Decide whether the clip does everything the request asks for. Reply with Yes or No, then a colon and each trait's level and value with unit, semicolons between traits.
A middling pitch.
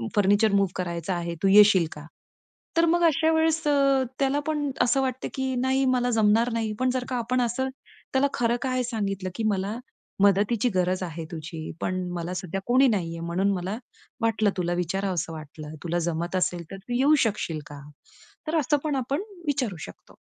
No: high, 210 Hz